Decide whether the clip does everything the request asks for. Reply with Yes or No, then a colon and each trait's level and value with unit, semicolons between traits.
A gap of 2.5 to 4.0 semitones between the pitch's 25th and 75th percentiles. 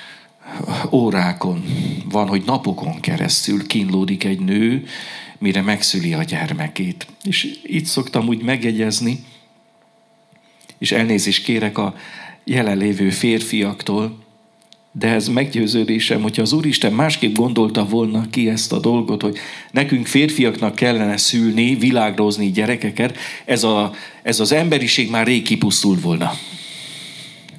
No: wide, 6.4 semitones